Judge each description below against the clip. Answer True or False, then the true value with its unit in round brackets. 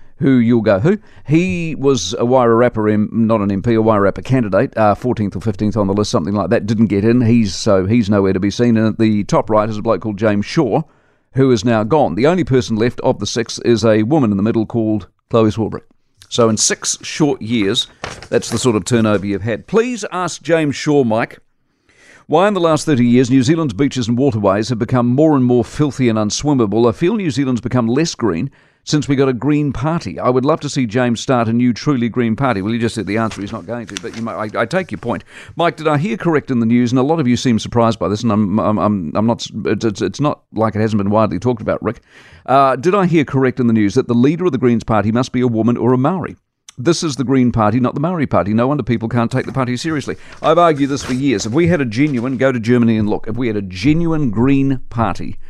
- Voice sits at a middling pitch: False (120 Hz)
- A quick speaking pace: True (260 wpm)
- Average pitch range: True (3.8 semitones)